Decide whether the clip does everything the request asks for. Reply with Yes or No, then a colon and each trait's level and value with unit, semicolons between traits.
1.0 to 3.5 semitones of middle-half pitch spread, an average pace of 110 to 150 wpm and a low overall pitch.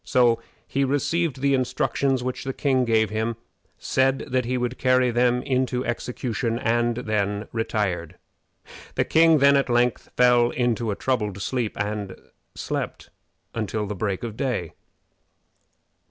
Yes: average, 2.8 semitones; average, 140 wpm; low, 120 Hz